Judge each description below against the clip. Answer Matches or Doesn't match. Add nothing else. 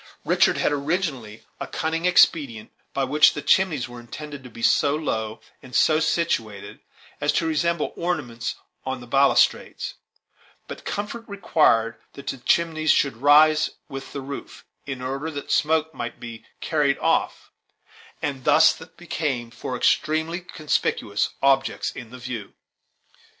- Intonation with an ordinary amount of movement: Matches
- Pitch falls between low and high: Matches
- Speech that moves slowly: Doesn't match